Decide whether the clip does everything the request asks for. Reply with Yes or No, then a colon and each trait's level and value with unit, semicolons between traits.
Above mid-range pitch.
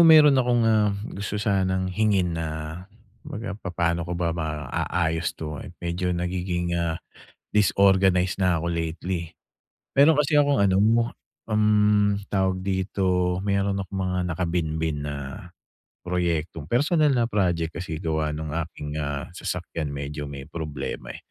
No: very low, 90 Hz